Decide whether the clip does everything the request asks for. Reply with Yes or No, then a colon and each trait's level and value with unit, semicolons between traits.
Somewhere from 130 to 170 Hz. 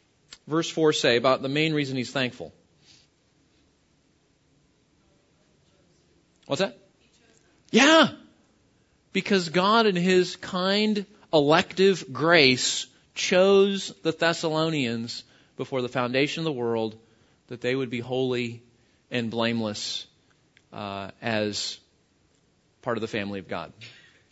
Yes: low, 135 Hz